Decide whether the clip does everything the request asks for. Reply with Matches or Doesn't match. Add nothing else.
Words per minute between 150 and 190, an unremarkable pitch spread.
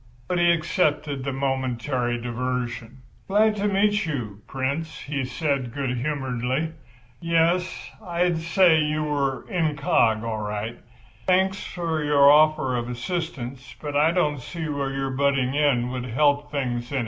Doesn't match